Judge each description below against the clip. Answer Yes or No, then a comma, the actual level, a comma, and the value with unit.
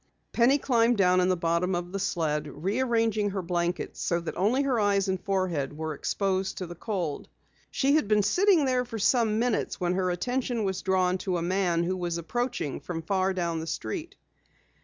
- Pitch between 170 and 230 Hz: Yes, high, 190 Hz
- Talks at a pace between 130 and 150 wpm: No, average, 195 wpm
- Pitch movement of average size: Yes, average, 4.5 semitones